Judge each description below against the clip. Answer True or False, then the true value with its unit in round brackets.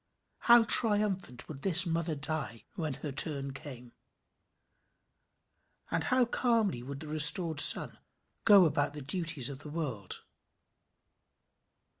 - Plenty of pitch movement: False (5.0 semitones)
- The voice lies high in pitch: False (155 Hz)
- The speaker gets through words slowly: True (120 wpm)